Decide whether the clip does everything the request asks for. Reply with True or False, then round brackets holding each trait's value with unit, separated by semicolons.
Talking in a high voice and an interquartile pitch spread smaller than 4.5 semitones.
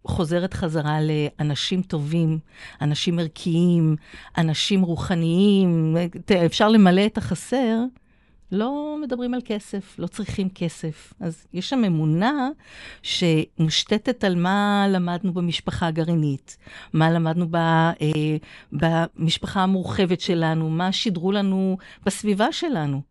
False (180 Hz; 3.7 semitones)